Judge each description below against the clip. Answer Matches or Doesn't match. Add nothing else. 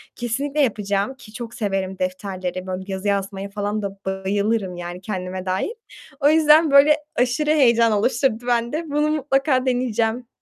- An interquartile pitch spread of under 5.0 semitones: Doesn't match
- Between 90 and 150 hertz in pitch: Doesn't match